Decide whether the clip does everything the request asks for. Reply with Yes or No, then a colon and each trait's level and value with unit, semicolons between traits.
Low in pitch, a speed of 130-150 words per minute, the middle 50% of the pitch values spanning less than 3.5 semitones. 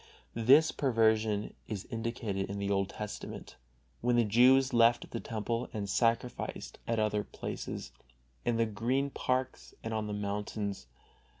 Yes: low, 115 Hz; average, 140 wpm; narrow, 2.6 semitones